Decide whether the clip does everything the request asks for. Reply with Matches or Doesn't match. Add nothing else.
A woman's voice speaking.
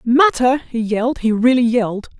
Matches